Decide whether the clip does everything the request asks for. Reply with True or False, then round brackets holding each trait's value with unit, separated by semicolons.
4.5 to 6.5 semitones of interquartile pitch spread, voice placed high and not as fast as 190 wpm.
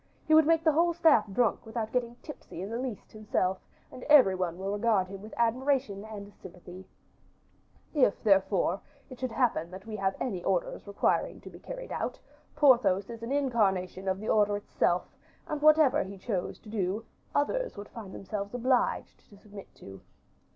True (4.9 semitones; 215 Hz; 180 wpm)